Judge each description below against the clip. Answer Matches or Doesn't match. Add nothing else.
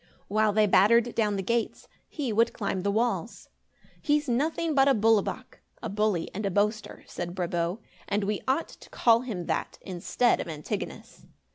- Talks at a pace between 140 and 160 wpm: Doesn't match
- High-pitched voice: Matches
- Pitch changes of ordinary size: Matches